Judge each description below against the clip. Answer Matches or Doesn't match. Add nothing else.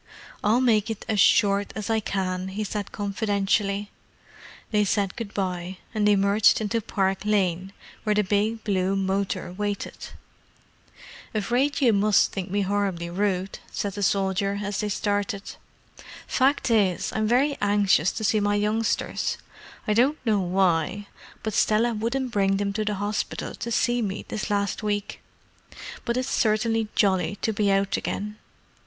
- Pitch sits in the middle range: Doesn't match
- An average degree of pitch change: Doesn't match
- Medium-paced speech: Matches